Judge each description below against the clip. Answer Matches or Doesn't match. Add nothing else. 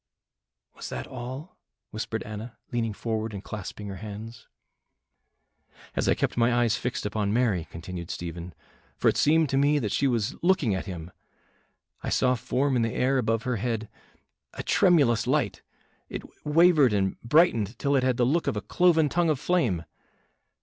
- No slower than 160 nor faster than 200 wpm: Matches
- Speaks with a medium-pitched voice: Doesn't match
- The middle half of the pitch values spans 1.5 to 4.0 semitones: Doesn't match